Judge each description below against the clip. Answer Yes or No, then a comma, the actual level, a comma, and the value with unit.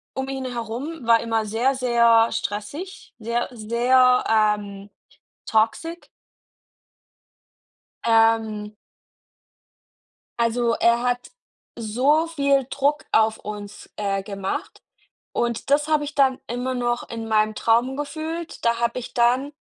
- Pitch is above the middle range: Yes, high, 235 Hz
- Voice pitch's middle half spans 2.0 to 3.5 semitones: Yes, average, 3.2 semitones